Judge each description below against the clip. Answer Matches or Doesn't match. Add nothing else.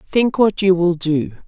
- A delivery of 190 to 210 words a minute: Matches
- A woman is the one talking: Matches